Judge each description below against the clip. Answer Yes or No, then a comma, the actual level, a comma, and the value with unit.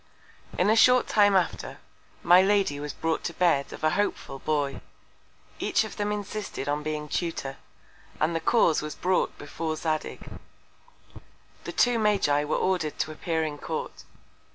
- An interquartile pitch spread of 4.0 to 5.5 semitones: Yes, average, 5.0 semitones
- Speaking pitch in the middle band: Yes, medium, 165 Hz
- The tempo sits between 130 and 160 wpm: Yes, average, 155 wpm